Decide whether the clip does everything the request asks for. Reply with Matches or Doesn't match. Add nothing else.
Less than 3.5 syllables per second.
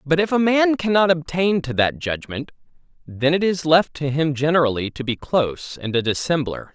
Doesn't match